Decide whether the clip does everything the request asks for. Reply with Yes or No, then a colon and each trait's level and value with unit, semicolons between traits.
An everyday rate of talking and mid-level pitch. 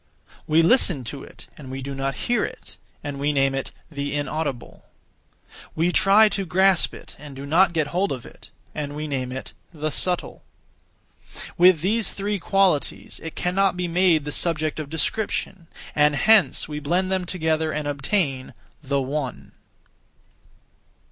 Yes: average, 160 wpm; medium, 155 Hz